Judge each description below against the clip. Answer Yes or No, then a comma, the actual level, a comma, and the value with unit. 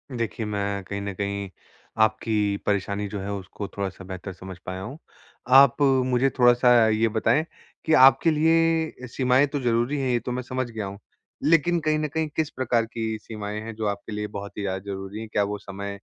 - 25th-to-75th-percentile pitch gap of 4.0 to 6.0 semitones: Yes, average, 4.4 semitones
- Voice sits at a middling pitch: No, low, 110 Hz